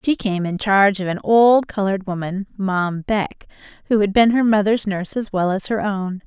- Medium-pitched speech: No, high, 200 Hz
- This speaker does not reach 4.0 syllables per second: No, 5.0 syllables/s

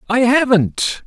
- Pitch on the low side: No, high, 230 Hz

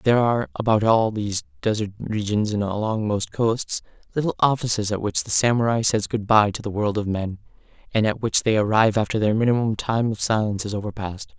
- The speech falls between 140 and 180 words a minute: No, average, 200 wpm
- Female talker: No, male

